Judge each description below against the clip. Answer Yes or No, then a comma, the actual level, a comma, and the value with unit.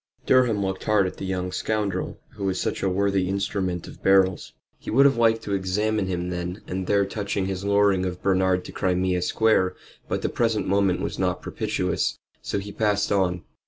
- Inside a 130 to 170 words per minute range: No, average, 195 wpm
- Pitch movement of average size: No, narrow, 1.9 semitones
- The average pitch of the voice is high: No, very low, 95 Hz